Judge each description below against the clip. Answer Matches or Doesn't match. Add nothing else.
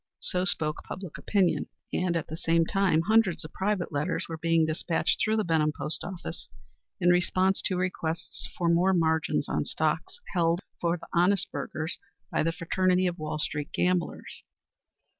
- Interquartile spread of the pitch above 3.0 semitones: Doesn't match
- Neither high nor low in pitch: Matches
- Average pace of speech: Matches